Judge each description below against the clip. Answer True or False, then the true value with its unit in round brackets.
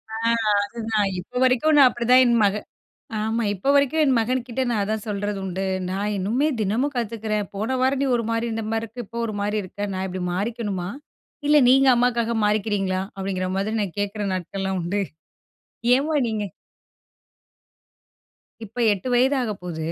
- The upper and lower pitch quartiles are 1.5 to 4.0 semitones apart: True (3.6 semitones)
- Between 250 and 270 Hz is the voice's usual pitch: False (220 Hz)